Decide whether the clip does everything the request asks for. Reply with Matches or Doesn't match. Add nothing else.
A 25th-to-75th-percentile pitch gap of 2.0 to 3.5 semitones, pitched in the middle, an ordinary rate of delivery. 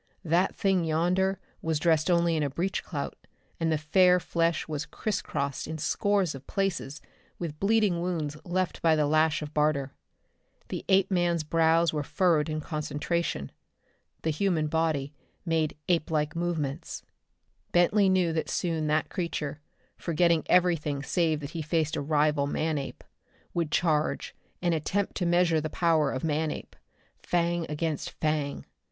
Matches